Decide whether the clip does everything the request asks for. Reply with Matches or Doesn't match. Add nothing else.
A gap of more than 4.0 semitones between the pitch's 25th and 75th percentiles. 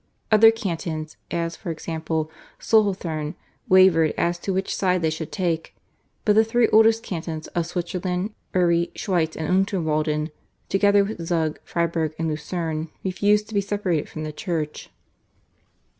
Doesn't match